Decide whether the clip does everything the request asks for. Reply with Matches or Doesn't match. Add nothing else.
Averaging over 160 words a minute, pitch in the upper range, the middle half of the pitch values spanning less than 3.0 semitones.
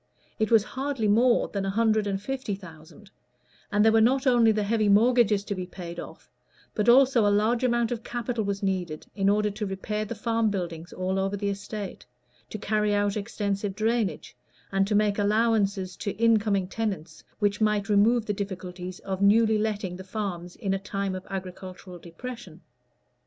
Matches